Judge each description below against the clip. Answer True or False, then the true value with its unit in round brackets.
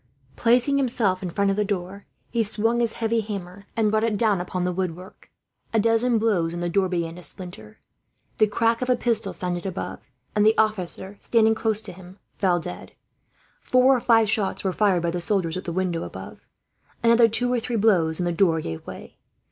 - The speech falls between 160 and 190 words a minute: False (205 wpm)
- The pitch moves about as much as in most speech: True (4.1 semitones)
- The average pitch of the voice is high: True (200 Hz)